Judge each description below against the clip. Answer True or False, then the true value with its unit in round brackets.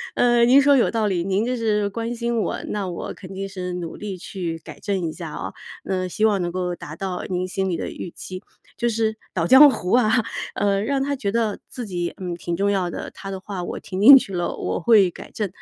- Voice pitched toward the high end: True (195 Hz)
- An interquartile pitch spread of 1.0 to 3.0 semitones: False (4.0 semitones)